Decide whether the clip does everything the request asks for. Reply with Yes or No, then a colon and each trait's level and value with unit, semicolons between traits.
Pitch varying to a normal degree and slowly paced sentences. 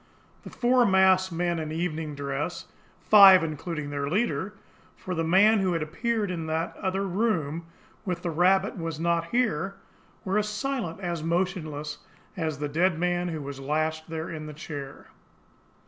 No: average, 3.4 semitones; average, 165 wpm